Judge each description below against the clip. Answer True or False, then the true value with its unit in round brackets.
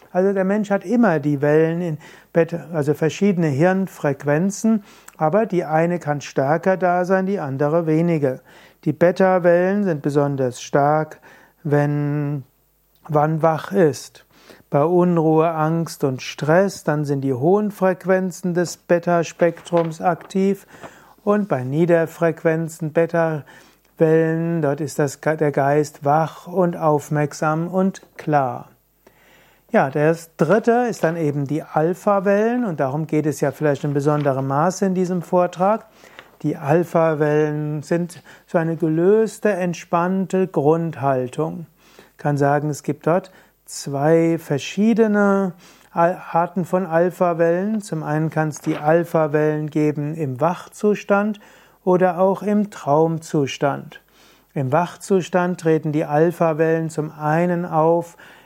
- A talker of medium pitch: True (165 Hz)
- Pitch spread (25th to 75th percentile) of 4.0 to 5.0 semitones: False (3.4 semitones)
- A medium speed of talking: False (120 wpm)